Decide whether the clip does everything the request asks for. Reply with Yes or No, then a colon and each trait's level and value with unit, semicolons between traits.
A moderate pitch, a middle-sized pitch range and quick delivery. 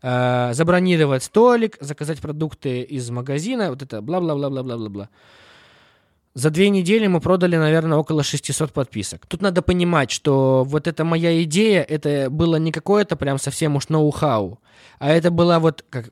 Yes: medium, 155 Hz; average, 4.2 semitones; fast, 165 wpm